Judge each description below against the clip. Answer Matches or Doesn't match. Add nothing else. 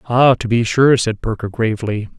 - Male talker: Matches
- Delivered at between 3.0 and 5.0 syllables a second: Doesn't match